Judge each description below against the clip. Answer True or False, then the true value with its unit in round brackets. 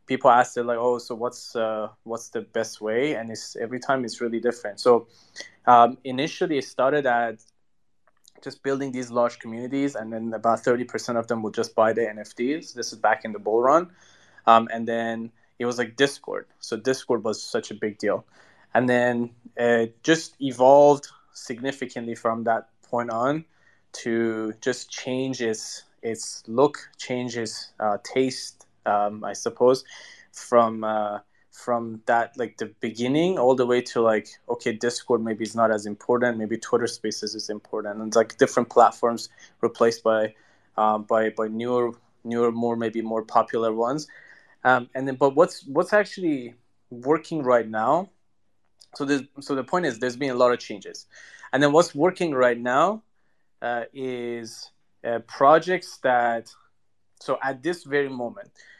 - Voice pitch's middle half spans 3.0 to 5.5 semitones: False (2.4 semitones)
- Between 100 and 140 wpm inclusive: False (165 wpm)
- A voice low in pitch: True (120 Hz)